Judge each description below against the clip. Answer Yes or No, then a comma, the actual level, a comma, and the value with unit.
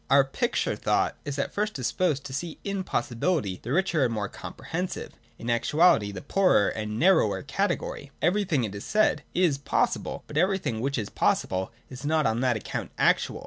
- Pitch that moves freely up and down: Yes, wide, 7.4 semitones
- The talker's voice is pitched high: No, medium, 140 Hz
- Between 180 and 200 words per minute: Yes, average, 185 wpm